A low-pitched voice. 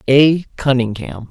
Yes: low, 130 Hz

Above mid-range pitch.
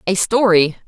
Yes: high, 195 Hz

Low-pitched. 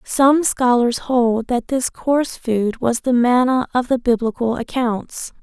No: high, 245 Hz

